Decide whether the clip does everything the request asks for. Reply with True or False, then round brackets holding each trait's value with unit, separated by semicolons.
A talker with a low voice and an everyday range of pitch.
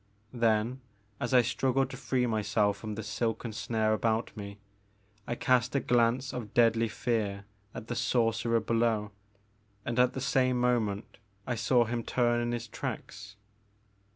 False (115 Hz; 2.1 semitones)